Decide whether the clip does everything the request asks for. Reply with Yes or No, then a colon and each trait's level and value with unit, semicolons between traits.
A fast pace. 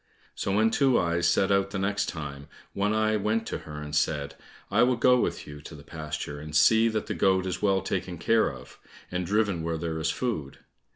Yes: fast, 220 wpm